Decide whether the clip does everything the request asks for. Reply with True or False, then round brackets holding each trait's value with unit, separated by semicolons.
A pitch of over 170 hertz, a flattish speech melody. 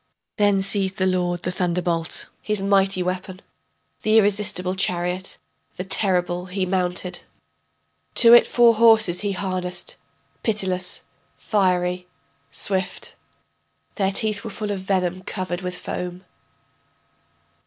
True (185 Hz; 2.0 semitones)